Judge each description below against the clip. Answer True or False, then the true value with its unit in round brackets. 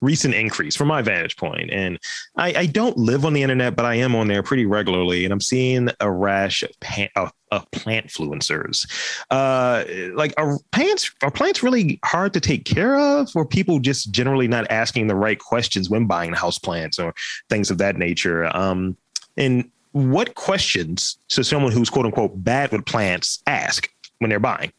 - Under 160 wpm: False (190 wpm)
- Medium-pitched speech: False (120 Hz)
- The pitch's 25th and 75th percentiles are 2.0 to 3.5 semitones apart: False (5.2 semitones)